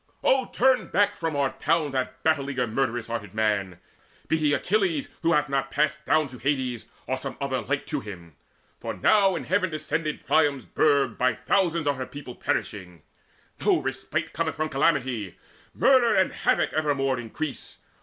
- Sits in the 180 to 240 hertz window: No, medium, 140 Hz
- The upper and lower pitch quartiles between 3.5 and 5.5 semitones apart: Yes, average, 3.8 semitones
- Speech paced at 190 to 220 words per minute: No, average, 170 wpm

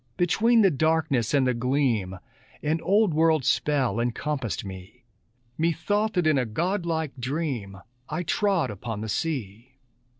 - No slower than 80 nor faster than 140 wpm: Yes, slow, 135 wpm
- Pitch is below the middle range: No, medium, 145 Hz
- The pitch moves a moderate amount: No, wide, 5.9 semitones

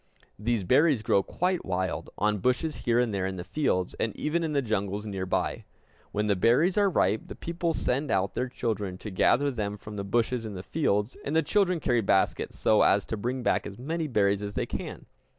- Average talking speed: No, fast, 220 wpm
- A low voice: Yes, low, 110 Hz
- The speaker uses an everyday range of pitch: No, wide, 6.2 semitones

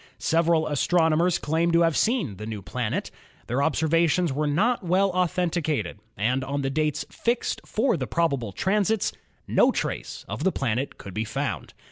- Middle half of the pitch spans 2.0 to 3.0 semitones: No, average, 5.0 semitones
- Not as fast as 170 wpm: Yes, average, 160 wpm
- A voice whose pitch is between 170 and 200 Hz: No, medium, 160 Hz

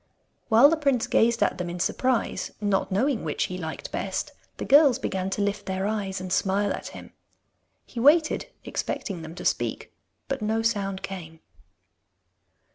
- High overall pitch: Yes, high, 205 Hz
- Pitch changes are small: No, average, 4.3 semitones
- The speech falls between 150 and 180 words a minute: Yes, average, 165 wpm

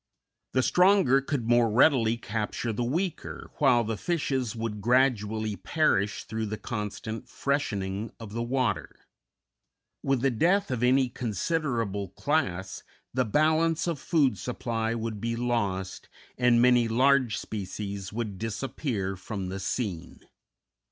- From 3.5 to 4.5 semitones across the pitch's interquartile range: Yes, average, 4.1 semitones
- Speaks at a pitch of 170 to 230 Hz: No, low, 115 Hz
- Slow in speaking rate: Yes, slow, 130 wpm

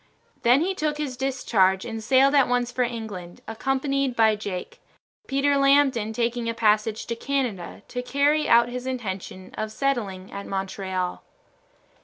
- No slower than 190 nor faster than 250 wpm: No, average, 150 wpm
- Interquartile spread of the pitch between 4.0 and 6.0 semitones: Yes, average, 4.5 semitones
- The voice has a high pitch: Yes, high, 235 Hz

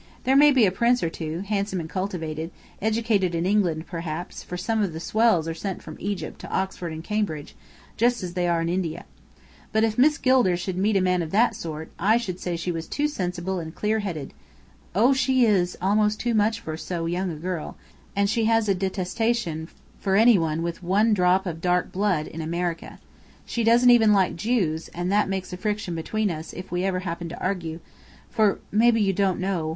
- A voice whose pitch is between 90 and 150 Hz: No, medium, 185 Hz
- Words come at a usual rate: No, fast, 210 wpm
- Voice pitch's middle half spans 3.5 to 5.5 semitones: Yes, average, 4.0 semitones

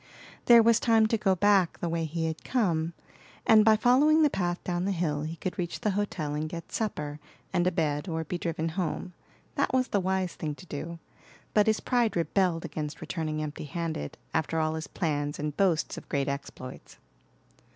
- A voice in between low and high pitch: Yes, medium, 170 Hz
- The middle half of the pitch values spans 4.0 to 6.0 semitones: Yes, average, 4.3 semitones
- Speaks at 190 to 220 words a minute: Yes, average, 195 wpm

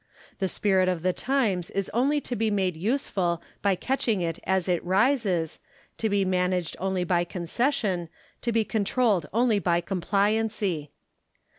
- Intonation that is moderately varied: Yes, average, 3.8 semitones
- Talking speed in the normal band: Yes, average, 150 wpm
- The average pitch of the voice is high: Yes, high, 195 Hz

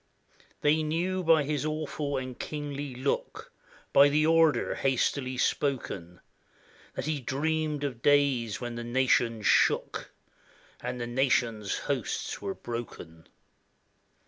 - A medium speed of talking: No, slow, 120 wpm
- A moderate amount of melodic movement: Yes, average, 3.9 semitones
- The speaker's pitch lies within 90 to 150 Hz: Yes, low, 135 Hz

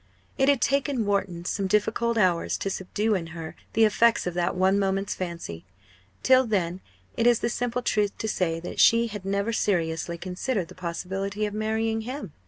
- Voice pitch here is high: Yes, high, 200 Hz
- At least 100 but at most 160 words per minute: No, average, 185 wpm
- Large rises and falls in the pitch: No, average, 3.8 semitones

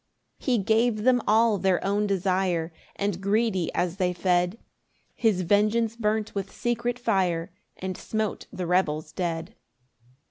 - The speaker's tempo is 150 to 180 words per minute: No, average, 140 wpm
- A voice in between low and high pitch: No, high, 195 Hz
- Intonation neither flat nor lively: Yes, average, 3.5 semitones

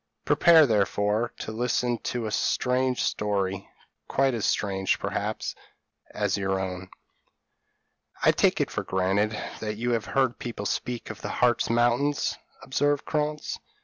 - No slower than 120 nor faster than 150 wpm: Yes, average, 140 wpm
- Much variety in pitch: No, average, 3.7 semitones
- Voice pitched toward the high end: No, low, 115 Hz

